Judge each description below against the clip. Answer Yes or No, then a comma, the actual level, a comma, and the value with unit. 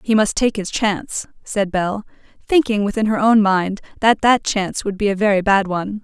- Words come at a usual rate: No, fast, 210 wpm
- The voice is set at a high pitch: Yes, high, 205 Hz